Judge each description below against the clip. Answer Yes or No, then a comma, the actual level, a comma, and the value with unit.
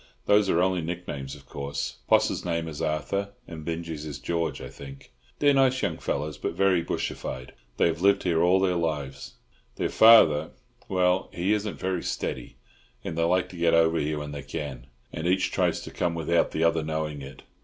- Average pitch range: Yes, average, 3.6 semitones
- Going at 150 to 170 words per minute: No, average, 195 wpm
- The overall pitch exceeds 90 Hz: No, very low, 85 Hz